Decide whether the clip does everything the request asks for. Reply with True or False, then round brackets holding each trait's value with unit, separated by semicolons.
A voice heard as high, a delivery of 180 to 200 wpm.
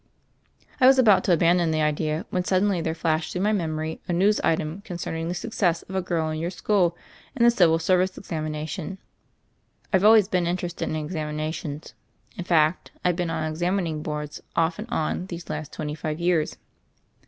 False (170 Hz; 190 wpm)